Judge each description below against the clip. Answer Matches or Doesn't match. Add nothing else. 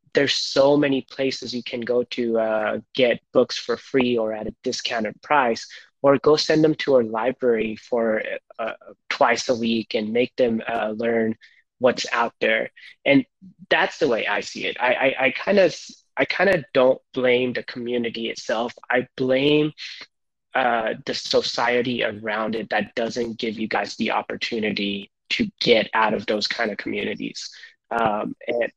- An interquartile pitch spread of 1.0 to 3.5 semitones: Matches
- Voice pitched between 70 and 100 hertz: Doesn't match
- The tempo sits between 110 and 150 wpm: Doesn't match